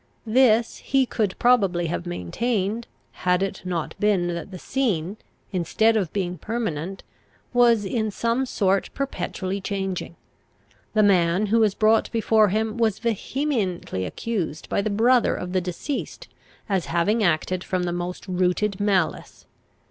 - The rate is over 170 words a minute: No, average, 140 wpm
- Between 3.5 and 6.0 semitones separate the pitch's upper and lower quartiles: Yes, average, 3.9 semitones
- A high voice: Yes, high, 200 Hz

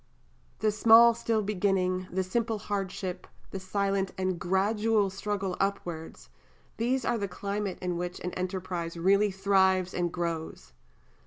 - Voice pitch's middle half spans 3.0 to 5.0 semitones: No, narrow, 2.4 semitones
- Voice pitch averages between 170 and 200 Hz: Yes, high, 190 Hz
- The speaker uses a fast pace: No, slow, 135 wpm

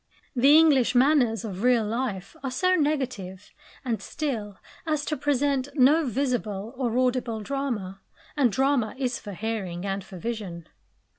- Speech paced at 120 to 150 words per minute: Yes, average, 145 wpm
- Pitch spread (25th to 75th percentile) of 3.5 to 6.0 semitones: Yes, average, 4.9 semitones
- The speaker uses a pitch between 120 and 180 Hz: No, high, 245 Hz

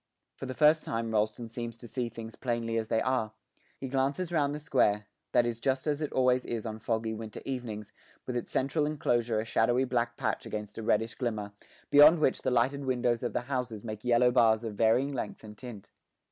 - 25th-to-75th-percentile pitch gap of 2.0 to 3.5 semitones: Yes, average, 2.8 semitones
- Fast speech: Yes, fast, 210 wpm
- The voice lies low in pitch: Yes, low, 120 Hz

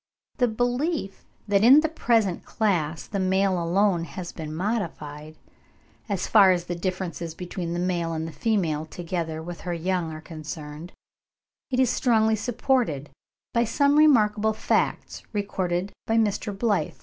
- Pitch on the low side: No, medium, 185 Hz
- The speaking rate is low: No, average, 150 wpm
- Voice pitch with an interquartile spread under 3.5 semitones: No, average, 4.8 semitones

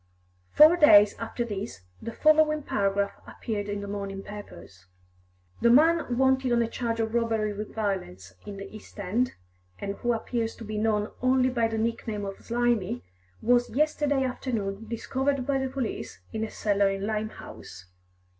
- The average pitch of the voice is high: Yes, high, 225 Hz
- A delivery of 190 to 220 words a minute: No, average, 165 wpm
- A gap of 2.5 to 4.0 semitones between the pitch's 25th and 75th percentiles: Yes, average, 3.7 semitones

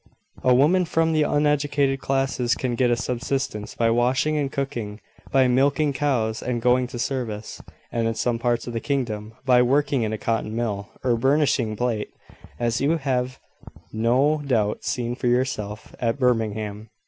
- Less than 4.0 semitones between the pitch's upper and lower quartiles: Yes, average, 3.2 semitones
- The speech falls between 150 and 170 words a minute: Yes, average, 165 wpm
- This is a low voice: Yes, low, 125 Hz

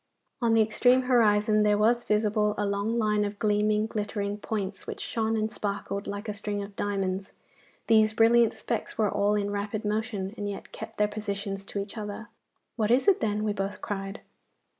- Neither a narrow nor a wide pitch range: No, narrow, 1.4 semitones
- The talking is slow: No, average, 185 wpm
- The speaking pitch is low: No, high, 210 Hz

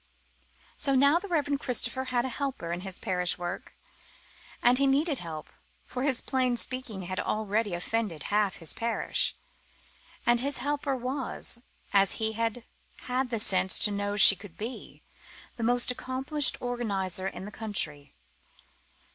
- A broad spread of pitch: No, average, 5.0 semitones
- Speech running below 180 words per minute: Yes, average, 150 wpm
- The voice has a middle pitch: No, high, 230 Hz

